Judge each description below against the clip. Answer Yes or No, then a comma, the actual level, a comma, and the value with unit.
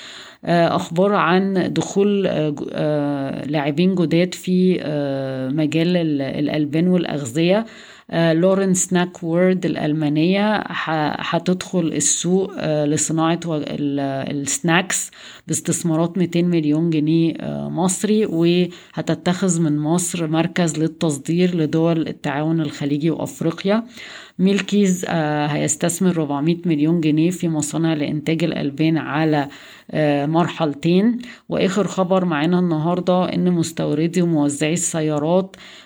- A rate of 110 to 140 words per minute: No, average, 85 wpm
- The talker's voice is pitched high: No, medium, 165 Hz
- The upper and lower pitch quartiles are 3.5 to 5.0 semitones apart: No, average, 2.9 semitones